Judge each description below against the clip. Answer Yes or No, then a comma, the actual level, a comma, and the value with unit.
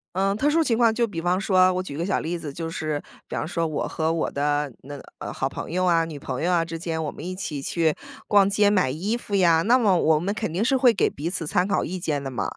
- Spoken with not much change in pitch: No, average, 4.1 semitones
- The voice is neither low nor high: Yes, medium, 175 Hz